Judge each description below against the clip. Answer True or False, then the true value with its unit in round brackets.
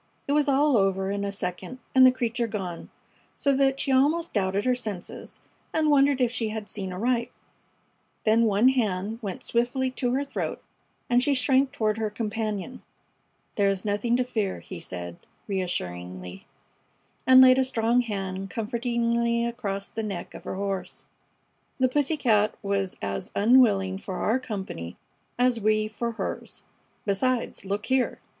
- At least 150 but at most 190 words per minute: True (160 wpm)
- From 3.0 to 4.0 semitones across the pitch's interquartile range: False (4.4 semitones)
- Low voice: False (225 Hz)